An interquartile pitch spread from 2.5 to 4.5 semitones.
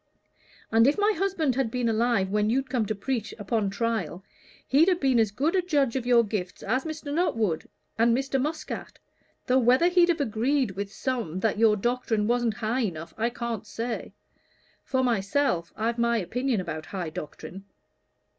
Yes: average, 4.1 semitones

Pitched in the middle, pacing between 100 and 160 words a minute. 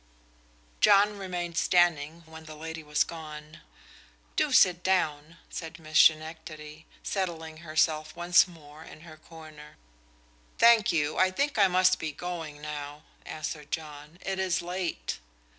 Yes: medium, 160 Hz; slow, 135 wpm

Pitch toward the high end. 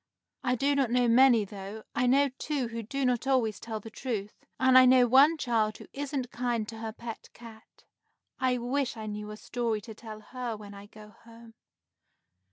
Yes: high, 235 Hz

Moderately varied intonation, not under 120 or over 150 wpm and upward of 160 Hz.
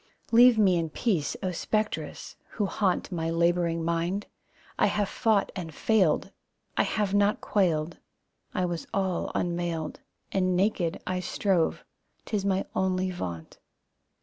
Yes: average, 3.1 semitones; slow, 135 wpm; medium, 185 Hz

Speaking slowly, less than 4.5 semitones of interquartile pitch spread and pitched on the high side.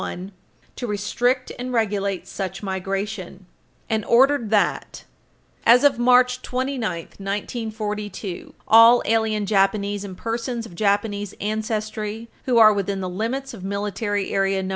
Yes: slow, 130 wpm; average, 2.8 semitones; high, 210 Hz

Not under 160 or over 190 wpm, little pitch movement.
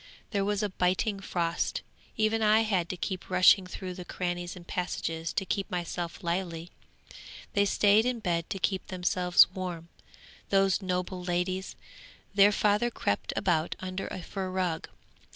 No: average, 150 wpm; narrow, 2.1 semitones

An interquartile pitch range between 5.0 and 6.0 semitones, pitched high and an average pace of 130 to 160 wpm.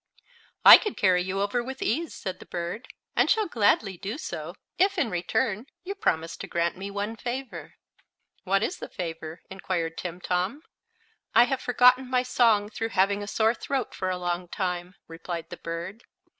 No: wide, 5.6 semitones; high, 200 Hz; average, 175 wpm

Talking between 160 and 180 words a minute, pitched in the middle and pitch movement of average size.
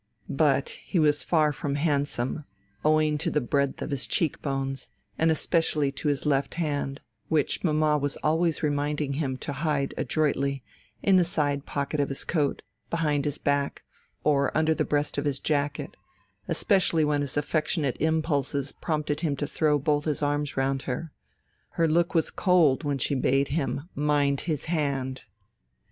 No: average, 165 wpm; medium, 145 Hz; narrow, 1.9 semitones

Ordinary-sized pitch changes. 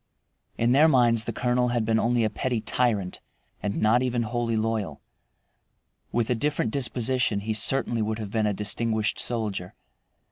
No: narrow, 2.1 semitones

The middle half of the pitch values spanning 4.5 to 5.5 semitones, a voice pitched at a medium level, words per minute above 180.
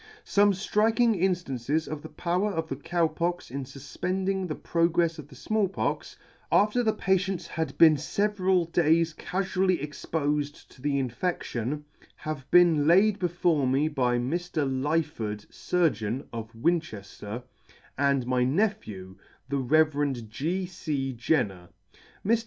No: average, 5.0 semitones; medium, 155 Hz; slow, 135 wpm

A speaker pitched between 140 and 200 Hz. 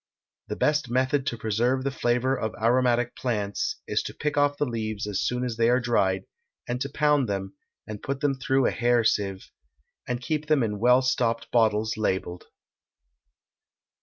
No: low, 120 Hz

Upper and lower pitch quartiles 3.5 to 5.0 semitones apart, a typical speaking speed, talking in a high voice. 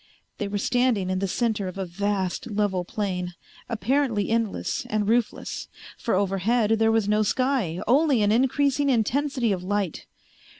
Yes: average, 3.8 semitones; average, 155 wpm; high, 210 Hz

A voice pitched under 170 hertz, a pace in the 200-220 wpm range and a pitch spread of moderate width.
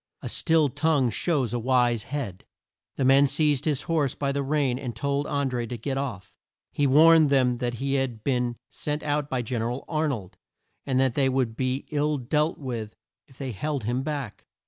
Yes: low, 135 Hz; fast, 205 wpm; average, 3.1 semitones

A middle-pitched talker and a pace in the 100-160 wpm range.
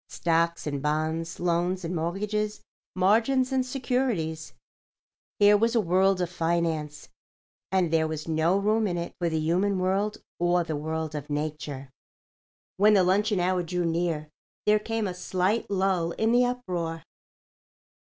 Yes: medium, 180 Hz; average, 145 wpm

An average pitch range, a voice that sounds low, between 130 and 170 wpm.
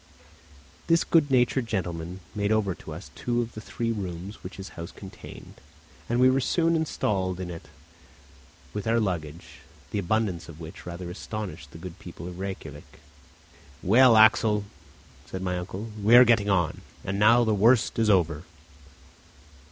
Yes: average, 4.5 semitones; low, 100 Hz; average, 165 wpm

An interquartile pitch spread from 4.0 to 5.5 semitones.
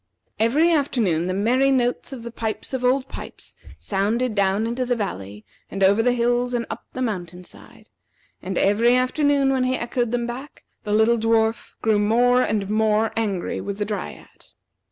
No: average, 3.3 semitones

